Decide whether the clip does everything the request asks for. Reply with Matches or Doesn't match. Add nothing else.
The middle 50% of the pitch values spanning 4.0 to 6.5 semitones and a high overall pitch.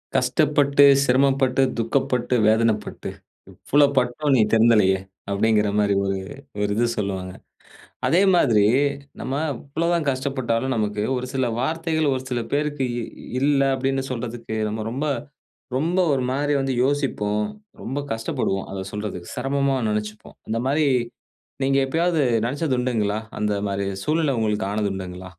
Doesn't match